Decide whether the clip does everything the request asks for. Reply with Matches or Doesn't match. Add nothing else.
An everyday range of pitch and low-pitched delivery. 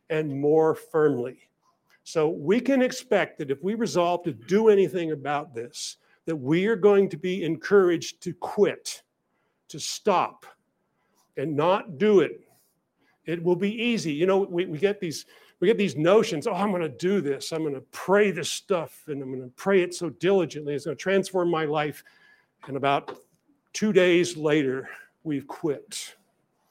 Doesn't match